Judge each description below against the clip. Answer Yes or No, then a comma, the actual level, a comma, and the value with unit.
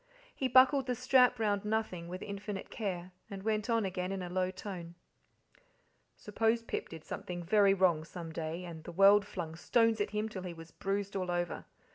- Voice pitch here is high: Yes, high, 195 Hz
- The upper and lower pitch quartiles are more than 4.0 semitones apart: No, average, 3.5 semitones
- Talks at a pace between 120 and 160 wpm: No, average, 190 wpm